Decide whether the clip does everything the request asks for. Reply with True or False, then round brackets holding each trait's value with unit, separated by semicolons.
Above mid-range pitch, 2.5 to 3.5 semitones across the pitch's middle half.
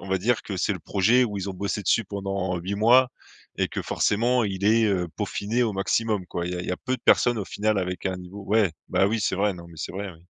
False (100 Hz; 2.9 semitones)